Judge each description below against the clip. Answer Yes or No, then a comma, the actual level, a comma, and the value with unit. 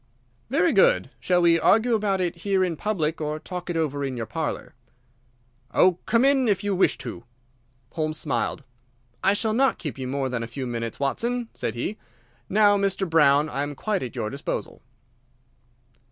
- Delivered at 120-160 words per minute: No, average, 180 wpm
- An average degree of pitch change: No, wide, 6.6 semitones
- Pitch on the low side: No, medium, 170 Hz